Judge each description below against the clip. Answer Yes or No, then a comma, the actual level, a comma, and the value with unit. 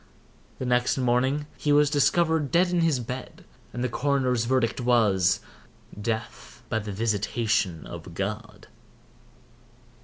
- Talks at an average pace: No, slow, 120 wpm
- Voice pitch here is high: No, low, 125 Hz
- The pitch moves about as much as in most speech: Yes, average, 4.2 semitones